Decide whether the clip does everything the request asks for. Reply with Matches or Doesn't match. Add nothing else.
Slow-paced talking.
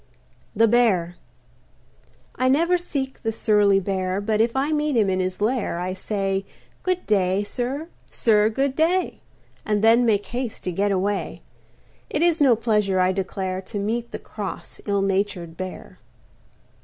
Doesn't match